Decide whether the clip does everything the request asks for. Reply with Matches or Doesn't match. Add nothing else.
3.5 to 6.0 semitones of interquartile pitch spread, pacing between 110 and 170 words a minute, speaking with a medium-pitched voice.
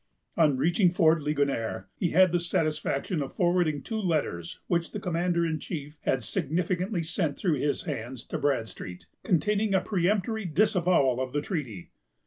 Matches